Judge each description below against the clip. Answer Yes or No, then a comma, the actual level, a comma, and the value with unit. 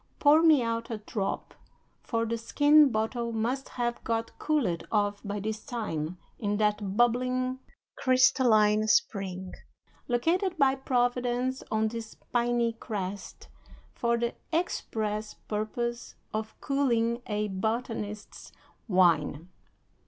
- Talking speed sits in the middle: No, slow, 115 wpm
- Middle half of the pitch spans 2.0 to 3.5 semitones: Yes, average, 3.1 semitones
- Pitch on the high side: Yes, high, 230 Hz